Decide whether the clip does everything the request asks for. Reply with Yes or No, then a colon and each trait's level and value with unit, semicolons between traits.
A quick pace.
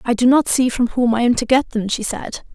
Yes: fast, 305 wpm